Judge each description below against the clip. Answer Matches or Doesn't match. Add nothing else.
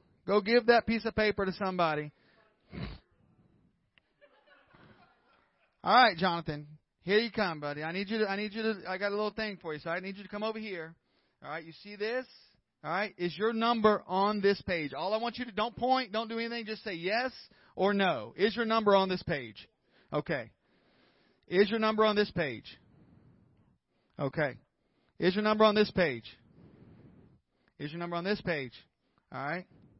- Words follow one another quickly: Doesn't match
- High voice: Matches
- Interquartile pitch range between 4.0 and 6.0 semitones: Matches